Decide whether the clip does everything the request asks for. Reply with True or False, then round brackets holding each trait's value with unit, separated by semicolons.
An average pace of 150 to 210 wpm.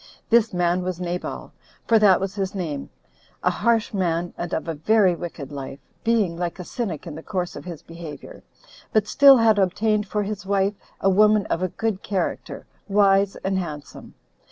True (180 wpm)